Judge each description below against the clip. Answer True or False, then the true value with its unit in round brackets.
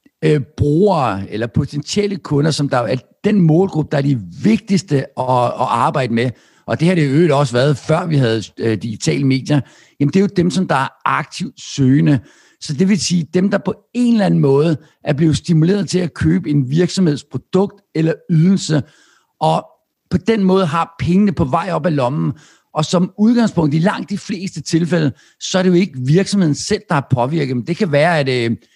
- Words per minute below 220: True (195 wpm)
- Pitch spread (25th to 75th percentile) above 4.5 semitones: True (5.0 semitones)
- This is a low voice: False (160 Hz)